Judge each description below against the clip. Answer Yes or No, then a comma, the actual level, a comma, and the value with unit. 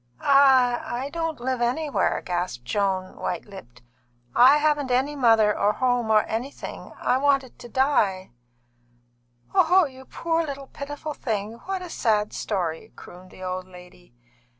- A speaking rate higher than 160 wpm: No, average, 145 wpm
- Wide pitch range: Yes, wide, 6.5 semitones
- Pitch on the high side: Yes, high, 245 Hz